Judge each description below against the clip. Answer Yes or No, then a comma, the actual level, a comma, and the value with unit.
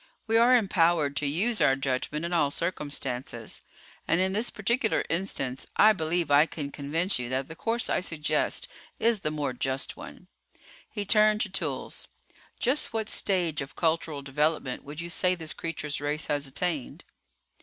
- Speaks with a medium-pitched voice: Yes, medium, 160 Hz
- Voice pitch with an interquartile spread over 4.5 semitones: Yes, average, 5.3 semitones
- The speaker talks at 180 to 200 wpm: No, average, 165 wpm